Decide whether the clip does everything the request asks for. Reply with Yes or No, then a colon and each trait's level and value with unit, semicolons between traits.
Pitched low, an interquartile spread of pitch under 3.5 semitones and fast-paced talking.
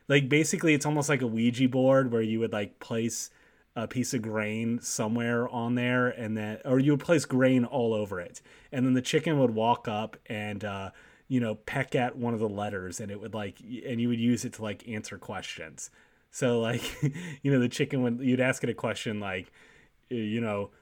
Yes: low, 120 Hz; average, 2.9 semitones; fast, 215 wpm